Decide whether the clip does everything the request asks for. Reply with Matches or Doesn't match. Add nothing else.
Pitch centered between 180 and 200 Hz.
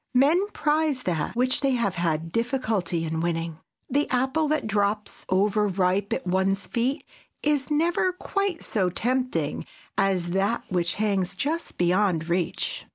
Doesn't match